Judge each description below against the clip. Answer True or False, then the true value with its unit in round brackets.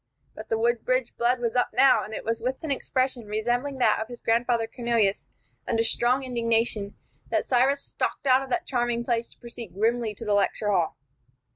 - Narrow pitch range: True (2.0 semitones)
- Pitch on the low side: False (235 Hz)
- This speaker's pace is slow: False (190 wpm)